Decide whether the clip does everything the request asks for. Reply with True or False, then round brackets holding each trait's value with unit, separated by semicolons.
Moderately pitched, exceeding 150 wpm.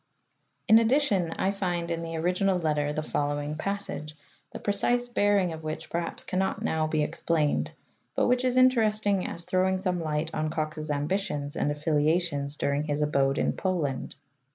True (165 Hz; 160 wpm)